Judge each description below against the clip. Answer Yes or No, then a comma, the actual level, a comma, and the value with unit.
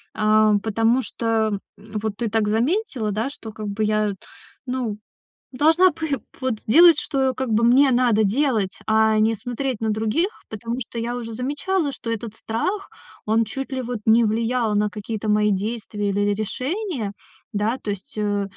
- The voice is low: No, high, 225 Hz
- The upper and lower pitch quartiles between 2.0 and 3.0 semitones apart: No, average, 3.4 semitones